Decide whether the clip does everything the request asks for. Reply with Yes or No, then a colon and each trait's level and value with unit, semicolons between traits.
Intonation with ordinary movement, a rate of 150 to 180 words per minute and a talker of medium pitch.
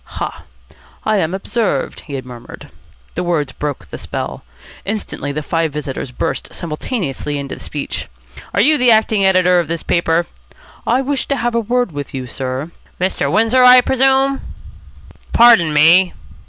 No: wide, 8.1 semitones; average, 155 wpm; medium, 175 Hz